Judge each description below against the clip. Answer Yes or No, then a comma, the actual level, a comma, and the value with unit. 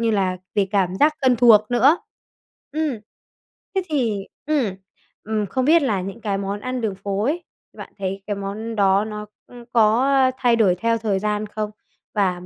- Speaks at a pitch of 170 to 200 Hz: No, high, 215 Hz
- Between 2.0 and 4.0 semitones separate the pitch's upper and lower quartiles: Yes, average, 3.6 semitones